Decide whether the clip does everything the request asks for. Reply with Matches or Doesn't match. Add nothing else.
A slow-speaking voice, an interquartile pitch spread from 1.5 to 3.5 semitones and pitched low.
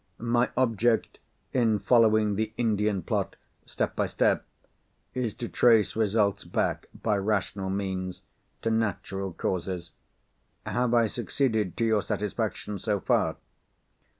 Matches